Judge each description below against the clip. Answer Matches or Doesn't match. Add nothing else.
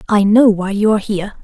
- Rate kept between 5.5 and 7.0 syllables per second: Matches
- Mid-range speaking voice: Doesn't match